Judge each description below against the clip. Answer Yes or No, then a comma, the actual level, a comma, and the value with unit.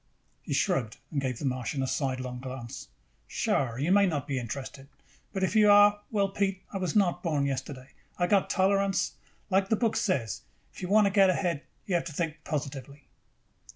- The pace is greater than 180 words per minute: Yes, average, 195 wpm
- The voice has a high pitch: No, medium, 165 Hz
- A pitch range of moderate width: No, wide, 6.5 semitones